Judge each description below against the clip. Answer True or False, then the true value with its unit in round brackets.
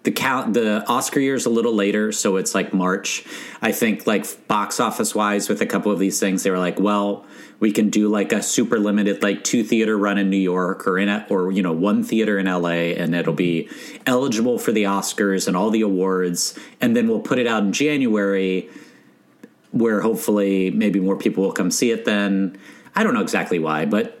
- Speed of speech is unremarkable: False (220 wpm)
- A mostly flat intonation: True (1.8 semitones)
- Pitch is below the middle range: True (100 Hz)